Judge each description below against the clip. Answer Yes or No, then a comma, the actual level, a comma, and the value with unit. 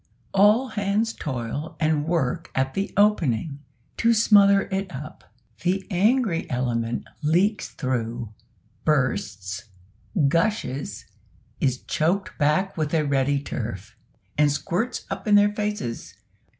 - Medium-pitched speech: Yes, medium, 160 Hz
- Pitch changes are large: Yes, wide, 7.4 semitones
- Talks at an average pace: No, slow, 115 wpm